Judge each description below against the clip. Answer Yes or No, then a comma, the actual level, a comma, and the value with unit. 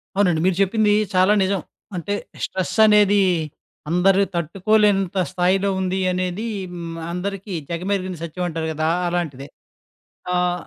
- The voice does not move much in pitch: Yes, narrow, 2.2 semitones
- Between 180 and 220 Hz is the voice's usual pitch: Yes, medium, 185 Hz